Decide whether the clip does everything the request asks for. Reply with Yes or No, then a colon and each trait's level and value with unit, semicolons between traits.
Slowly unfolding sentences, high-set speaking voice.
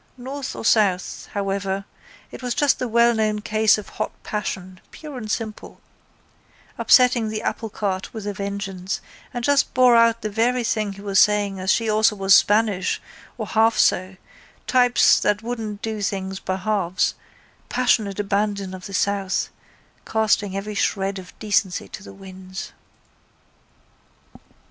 No: average, 145 wpm; high, 210 Hz